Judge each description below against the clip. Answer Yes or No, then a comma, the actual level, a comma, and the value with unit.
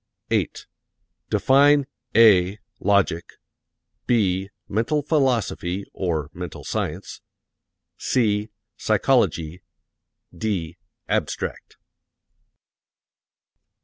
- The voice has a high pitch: No, low, 100 Hz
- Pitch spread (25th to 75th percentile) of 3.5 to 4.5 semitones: No, average, 5.1 semitones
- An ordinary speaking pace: No, slow, 60 wpm